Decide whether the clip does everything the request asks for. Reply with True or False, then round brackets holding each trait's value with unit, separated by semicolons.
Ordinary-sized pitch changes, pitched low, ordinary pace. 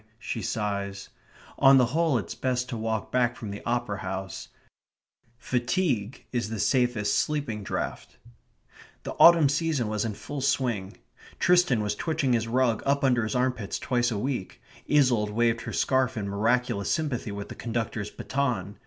True (3.8 semitones; 120 Hz; 160 wpm)